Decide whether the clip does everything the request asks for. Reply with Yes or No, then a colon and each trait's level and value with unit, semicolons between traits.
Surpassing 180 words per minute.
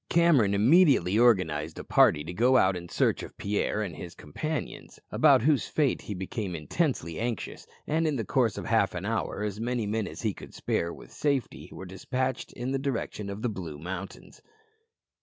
Yes: average, 190 wpm